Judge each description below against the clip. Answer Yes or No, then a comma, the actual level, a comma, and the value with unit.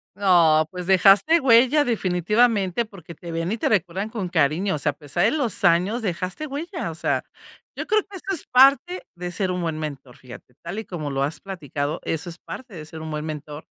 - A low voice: No, medium, 180 Hz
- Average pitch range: No, wide, 6.3 semitones